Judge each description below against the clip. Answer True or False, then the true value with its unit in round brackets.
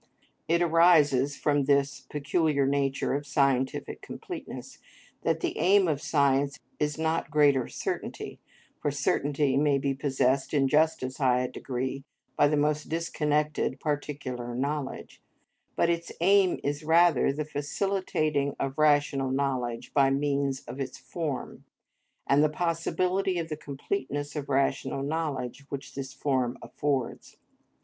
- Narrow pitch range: True (2.1 semitones)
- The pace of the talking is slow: True (130 wpm)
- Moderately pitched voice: True (145 Hz)